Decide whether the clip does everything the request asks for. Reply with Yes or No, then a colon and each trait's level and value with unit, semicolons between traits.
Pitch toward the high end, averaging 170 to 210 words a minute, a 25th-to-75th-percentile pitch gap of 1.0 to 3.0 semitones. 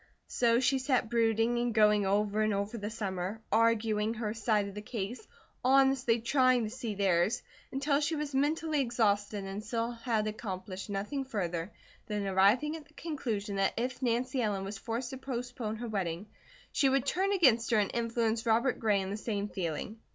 No: high, 225 Hz; average, 180 wpm; average, 3.6 semitones